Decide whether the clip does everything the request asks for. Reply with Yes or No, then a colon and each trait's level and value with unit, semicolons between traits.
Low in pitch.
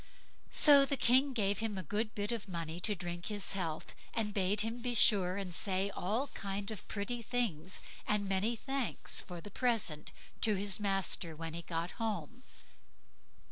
No: high, 205 Hz